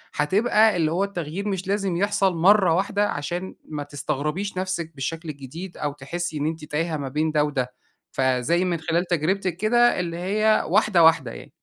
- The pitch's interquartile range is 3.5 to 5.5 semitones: Yes, average, 4.2 semitones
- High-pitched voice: No, medium, 170 Hz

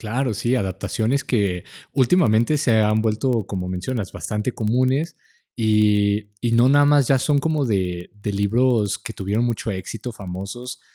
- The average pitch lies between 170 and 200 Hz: No, low, 110 Hz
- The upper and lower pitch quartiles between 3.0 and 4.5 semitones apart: Yes, average, 3.9 semitones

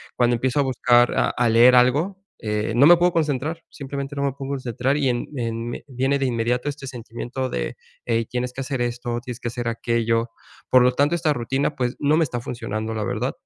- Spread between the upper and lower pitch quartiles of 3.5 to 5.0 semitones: No, average, 2.8 semitones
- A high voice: No, low, 125 Hz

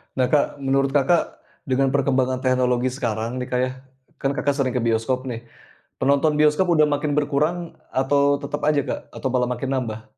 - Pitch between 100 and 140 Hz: Yes, low, 135 Hz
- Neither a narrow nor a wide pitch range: No, narrow, 2.2 semitones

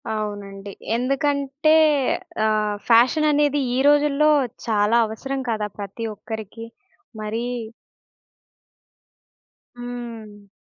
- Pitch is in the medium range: No, high, 230 Hz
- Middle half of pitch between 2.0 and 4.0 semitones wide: No, average, 4.8 semitones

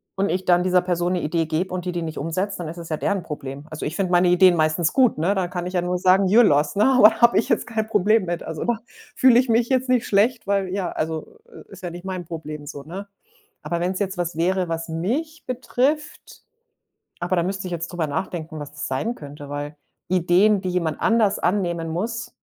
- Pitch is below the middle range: No, medium, 180 Hz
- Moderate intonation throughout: Yes, average, 3.7 semitones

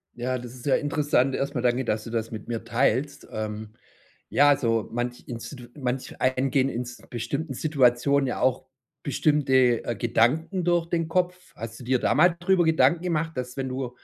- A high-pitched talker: No, low, 130 Hz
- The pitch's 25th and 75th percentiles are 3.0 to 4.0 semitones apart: Yes, average, 3.5 semitones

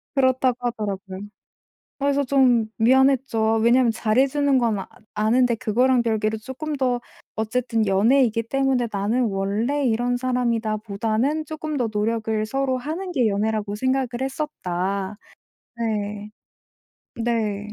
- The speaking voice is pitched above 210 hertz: Yes, high, 235 Hz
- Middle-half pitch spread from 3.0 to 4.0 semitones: Yes, average, 3.5 semitones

